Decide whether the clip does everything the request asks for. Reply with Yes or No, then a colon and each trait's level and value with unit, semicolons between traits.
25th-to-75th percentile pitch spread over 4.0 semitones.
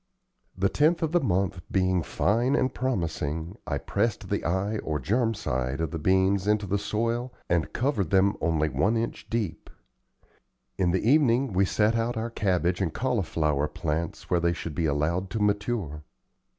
Yes: wide, 5.5 semitones